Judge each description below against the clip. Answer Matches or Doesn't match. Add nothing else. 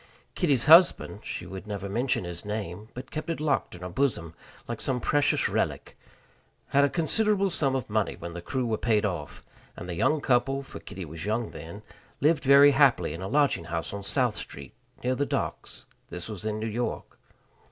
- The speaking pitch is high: Doesn't match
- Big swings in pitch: Matches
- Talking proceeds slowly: Doesn't match